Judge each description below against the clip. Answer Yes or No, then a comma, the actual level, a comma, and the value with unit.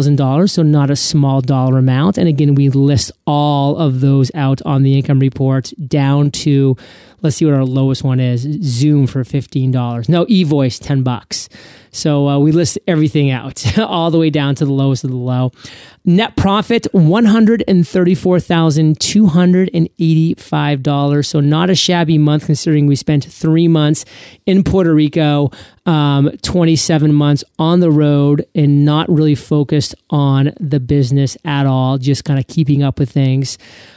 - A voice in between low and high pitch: Yes, medium, 145 Hz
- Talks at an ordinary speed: Yes, average, 155 wpm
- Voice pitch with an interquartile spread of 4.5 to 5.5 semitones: No, average, 2.9 semitones